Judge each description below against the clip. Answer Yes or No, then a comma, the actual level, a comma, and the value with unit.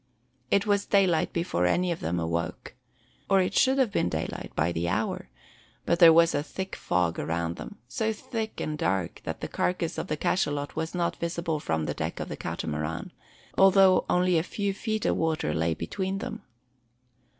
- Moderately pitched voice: Yes, medium, 165 Hz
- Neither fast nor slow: Yes, average, 185 wpm